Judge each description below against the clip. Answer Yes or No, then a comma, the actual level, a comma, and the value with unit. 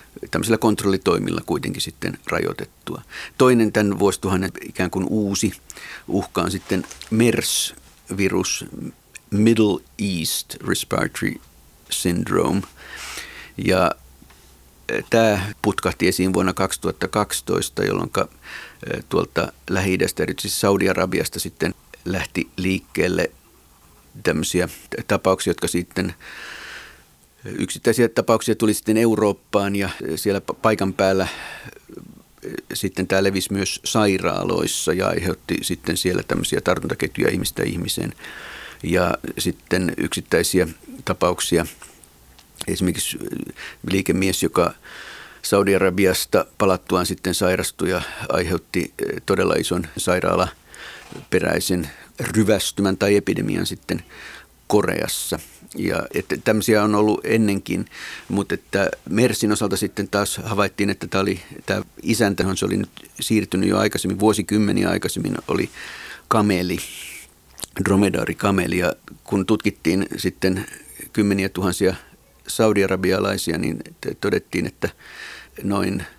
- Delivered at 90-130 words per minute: Yes, slow, 95 wpm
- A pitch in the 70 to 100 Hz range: Yes, very low, 95 Hz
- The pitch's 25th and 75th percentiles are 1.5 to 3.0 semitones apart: Yes, narrow, 2.4 semitones